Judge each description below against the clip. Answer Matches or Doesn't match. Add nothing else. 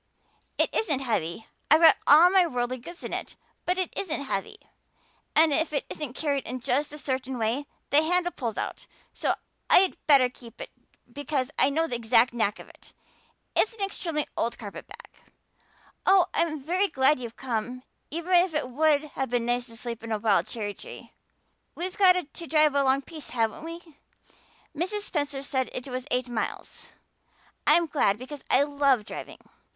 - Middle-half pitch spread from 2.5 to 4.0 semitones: Doesn't match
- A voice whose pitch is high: Matches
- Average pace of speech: Matches